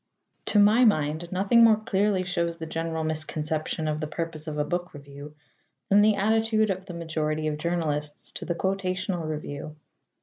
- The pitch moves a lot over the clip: No, average, 4.1 semitones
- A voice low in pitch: No, medium, 170 Hz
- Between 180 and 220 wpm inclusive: No, average, 170 wpm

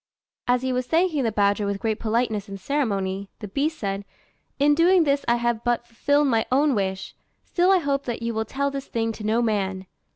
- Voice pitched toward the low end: No, high, 235 Hz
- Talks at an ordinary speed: No, fast, 215 wpm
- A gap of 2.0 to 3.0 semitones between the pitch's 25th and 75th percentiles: No, average, 5.1 semitones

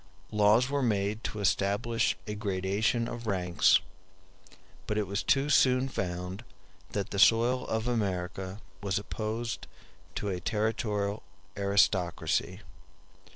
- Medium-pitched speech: No, low, 105 Hz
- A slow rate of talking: Yes, slow, 110 wpm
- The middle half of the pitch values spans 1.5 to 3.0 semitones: Yes, narrow, 2.6 semitones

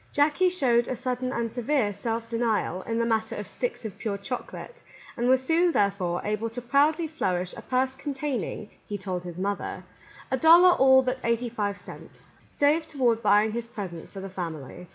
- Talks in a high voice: Yes, high, 235 Hz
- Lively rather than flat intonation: No, average, 4.5 semitones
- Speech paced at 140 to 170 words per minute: No, average, 185 wpm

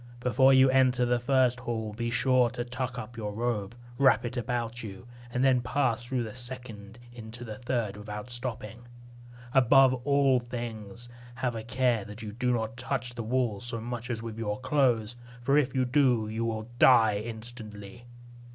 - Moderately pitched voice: No, low, 120 Hz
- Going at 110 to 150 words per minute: No, average, 180 wpm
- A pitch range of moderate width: No, narrow, 2.2 semitones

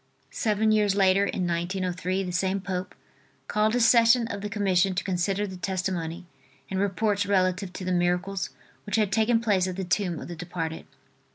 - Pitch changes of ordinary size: No, narrow, 2.3 semitones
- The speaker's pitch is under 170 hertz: No, high, 190 Hz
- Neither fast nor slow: Yes, average, 180 wpm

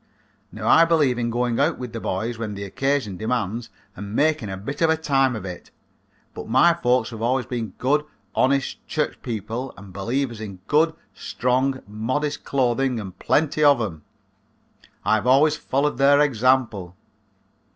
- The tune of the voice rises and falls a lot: No, average, 4.3 semitones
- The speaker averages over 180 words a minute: No, average, 165 wpm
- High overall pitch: No, low, 125 Hz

